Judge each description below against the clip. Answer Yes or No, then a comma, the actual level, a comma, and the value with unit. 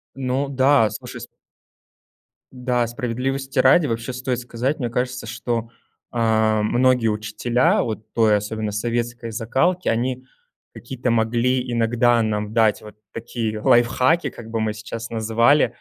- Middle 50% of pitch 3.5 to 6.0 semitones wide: No, narrow, 2.4 semitones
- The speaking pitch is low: Yes, low, 120 Hz